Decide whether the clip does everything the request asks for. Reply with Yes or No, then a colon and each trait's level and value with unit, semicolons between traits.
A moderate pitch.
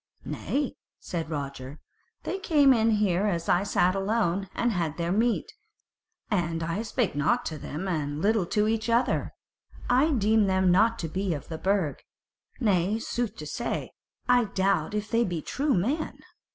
No: high, 195 Hz